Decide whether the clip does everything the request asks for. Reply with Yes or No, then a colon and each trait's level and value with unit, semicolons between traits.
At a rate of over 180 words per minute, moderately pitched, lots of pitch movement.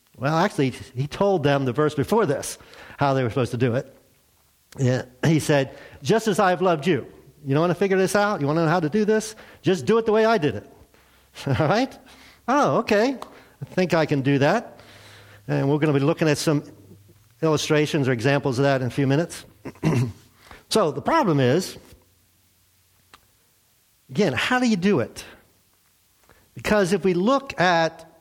Yes: average, 190 wpm; medium, 145 Hz; wide, 7.0 semitones